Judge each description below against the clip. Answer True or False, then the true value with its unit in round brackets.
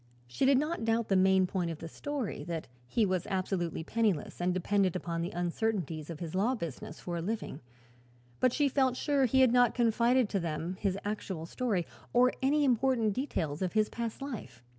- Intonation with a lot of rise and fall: True (6.2 semitones)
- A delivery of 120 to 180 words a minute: False (195 wpm)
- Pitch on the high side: True (200 Hz)